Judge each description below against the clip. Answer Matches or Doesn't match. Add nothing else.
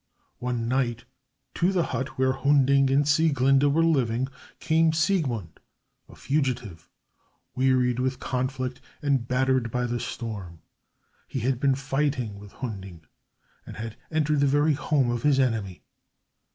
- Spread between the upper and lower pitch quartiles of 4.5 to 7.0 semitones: Doesn't match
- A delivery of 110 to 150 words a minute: Matches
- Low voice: Matches